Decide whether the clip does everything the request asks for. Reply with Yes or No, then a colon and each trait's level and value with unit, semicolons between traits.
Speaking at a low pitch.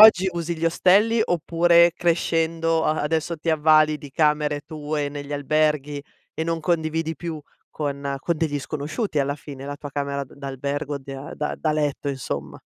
No: medium, 155 Hz